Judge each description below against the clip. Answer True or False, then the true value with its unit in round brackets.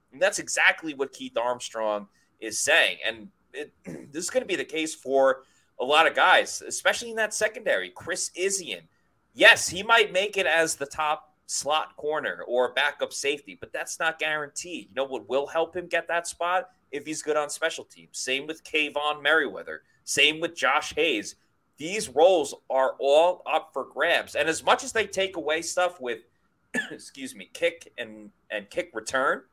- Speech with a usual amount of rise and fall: False (7.6 semitones)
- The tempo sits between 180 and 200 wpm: True (185 wpm)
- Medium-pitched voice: True (165 Hz)